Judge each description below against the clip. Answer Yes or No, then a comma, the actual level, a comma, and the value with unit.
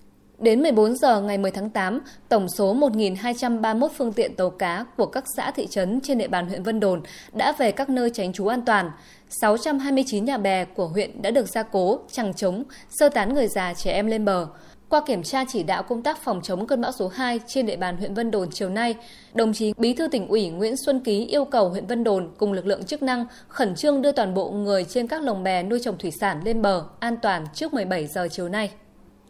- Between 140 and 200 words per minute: No, average, 235 wpm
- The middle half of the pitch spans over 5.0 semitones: No, average, 4.6 semitones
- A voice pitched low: No, high, 220 Hz